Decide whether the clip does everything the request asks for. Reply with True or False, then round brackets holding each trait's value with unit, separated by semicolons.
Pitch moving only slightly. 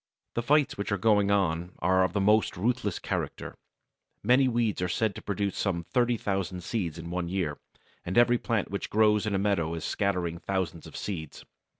False (3.5 semitones)